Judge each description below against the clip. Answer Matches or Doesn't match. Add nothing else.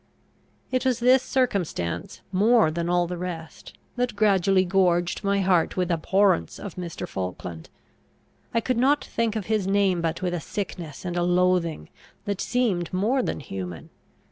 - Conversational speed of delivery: Matches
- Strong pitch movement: Doesn't match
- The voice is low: Doesn't match